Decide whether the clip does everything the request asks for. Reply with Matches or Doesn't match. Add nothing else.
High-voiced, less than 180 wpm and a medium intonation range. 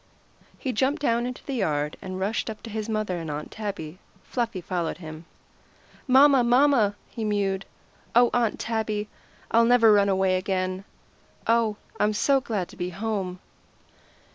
Matches